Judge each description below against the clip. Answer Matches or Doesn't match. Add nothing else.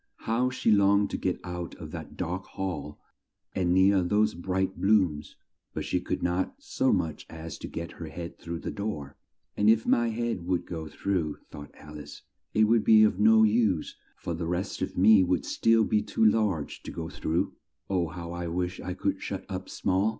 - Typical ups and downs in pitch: Matches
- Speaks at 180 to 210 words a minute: Matches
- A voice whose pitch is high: Doesn't match